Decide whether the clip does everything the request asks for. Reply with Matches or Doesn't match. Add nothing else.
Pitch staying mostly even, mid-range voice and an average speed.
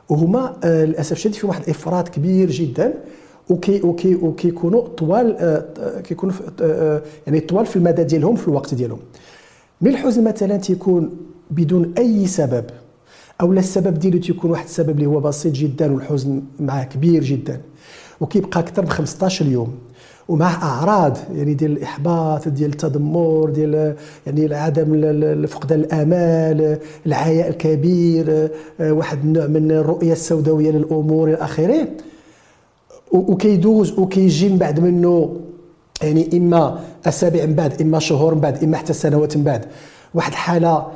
Doesn't match